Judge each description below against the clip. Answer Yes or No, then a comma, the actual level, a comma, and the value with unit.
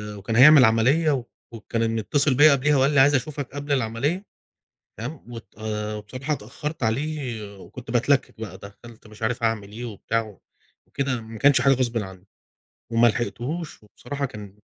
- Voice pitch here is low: Yes, low, 120 Hz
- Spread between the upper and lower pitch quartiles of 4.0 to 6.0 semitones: Yes, average, 4.3 semitones